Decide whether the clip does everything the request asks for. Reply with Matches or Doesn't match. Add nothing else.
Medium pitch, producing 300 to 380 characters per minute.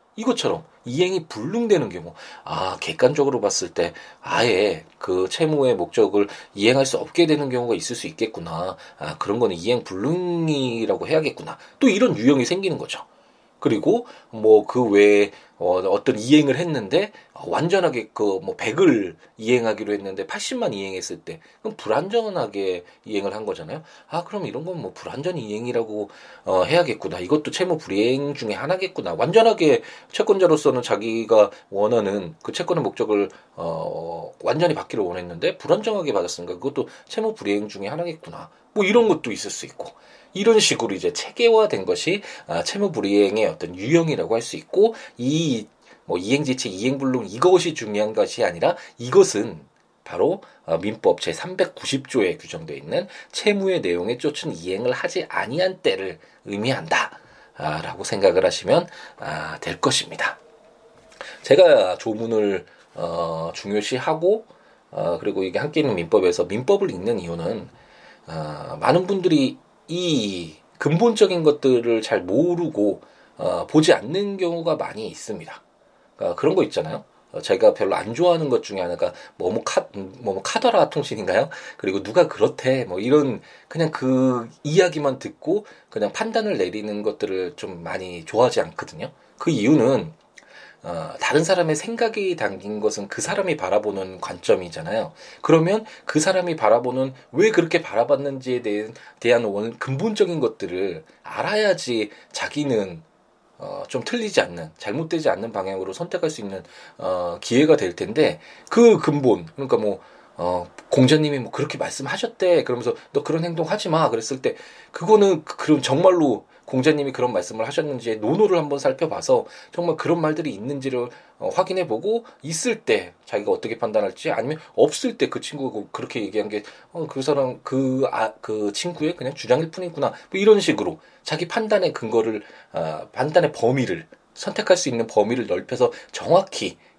Matches